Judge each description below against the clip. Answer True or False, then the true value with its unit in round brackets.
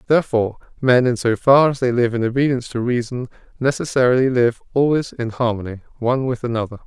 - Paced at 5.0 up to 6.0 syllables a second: False (6.4 syllables/s)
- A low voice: True (125 Hz)